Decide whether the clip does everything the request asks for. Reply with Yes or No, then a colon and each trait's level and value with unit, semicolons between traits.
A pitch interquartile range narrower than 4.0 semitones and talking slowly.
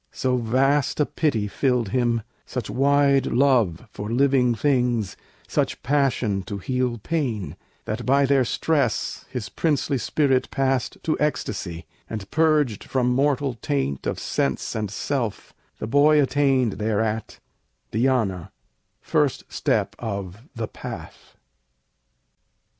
No: average, 4.3 semitones; slow, 120 wpm